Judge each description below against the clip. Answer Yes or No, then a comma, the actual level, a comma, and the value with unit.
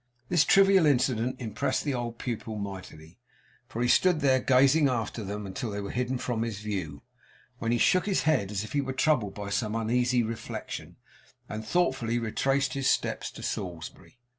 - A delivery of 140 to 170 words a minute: No, average, 180 wpm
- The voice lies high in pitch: No, low, 120 Hz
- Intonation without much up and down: No, average, 4.3 semitones